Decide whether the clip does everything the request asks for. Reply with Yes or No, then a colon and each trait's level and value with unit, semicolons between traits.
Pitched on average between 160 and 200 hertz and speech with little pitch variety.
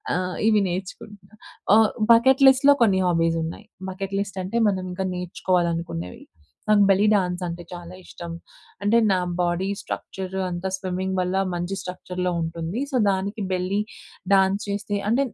Yes: high, 190 Hz; narrow, 2.3 semitones